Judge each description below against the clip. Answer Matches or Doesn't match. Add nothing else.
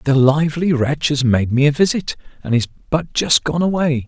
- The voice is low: Doesn't match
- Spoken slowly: Doesn't match